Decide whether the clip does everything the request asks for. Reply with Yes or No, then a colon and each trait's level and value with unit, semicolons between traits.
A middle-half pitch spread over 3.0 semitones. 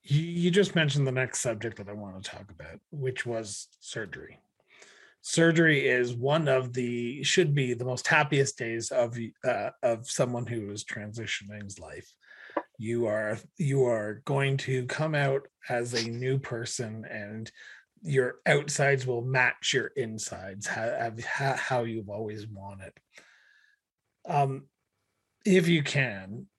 Yes: average, 4.2 semitones